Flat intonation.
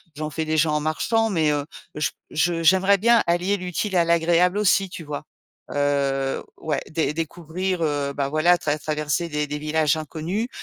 No: average, 3.1 semitones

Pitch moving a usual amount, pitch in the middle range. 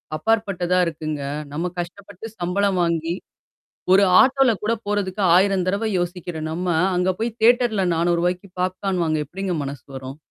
Yes: average, 3.0 semitones; medium, 180 Hz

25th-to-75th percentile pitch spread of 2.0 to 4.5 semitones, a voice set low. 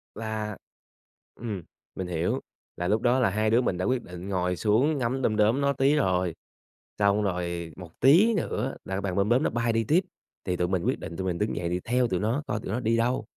No: average, 5.2 semitones; low, 105 Hz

